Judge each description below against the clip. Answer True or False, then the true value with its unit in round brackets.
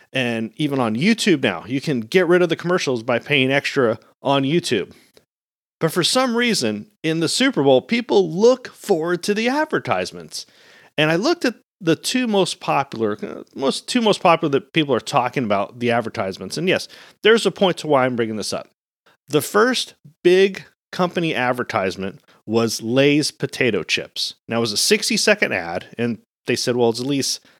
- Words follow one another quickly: False (185 wpm)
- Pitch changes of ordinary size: False (9.0 semitones)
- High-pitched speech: False (160 Hz)